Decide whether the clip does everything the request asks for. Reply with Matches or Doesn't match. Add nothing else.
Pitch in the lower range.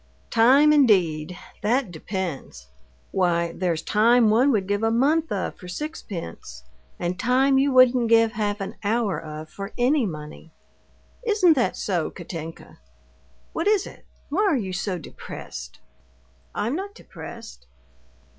Doesn't match